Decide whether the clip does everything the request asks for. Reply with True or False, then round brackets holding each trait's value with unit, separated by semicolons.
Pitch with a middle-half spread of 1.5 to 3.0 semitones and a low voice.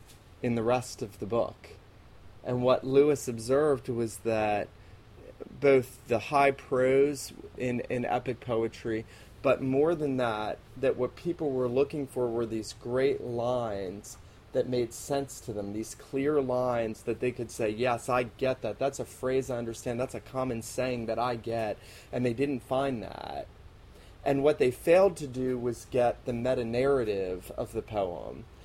True (2.6 semitones; 125 Hz)